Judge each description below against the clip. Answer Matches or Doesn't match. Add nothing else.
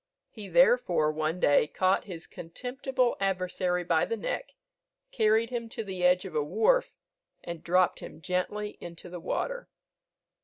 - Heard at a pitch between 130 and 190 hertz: Matches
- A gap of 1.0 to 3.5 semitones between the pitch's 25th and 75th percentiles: Doesn't match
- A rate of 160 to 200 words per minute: Doesn't match